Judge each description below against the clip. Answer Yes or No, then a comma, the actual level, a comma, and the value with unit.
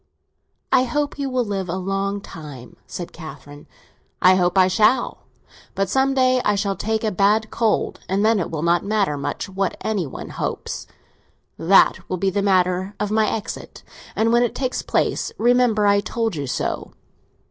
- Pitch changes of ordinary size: Yes, average, 3.4 semitones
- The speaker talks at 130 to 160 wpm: No, average, 180 wpm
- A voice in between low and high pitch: No, high, 200 Hz